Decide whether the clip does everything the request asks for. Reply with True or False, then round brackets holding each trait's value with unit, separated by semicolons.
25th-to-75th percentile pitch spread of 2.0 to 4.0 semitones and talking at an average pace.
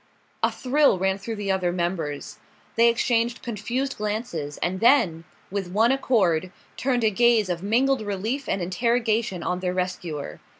False (4.7 semitones; 155 wpm)